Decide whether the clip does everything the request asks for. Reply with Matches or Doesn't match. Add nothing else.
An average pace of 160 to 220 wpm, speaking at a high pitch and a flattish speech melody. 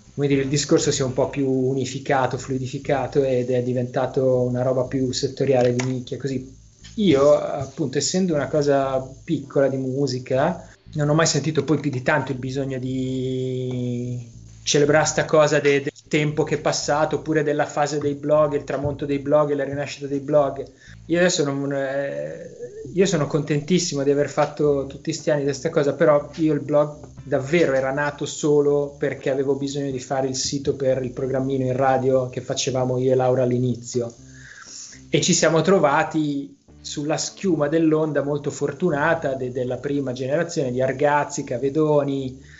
Doesn't match